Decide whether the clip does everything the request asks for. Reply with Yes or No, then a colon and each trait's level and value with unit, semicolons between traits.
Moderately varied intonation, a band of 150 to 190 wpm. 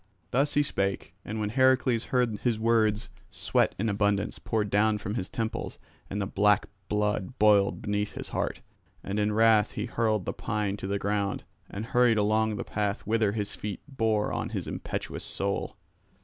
No: narrow, 1.7 semitones; average, 175 wpm